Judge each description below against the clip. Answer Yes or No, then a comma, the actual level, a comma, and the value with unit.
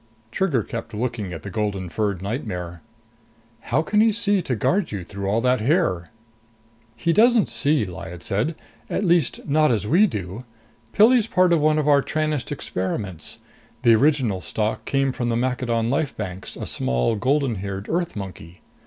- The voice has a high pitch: No, low, 120 Hz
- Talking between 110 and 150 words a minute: No, average, 170 wpm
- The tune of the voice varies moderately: No, wide, 7.6 semitones